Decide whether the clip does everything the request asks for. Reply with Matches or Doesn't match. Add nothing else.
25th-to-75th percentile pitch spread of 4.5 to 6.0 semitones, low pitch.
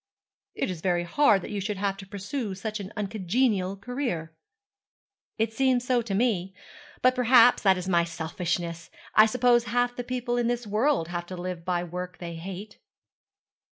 Doesn't match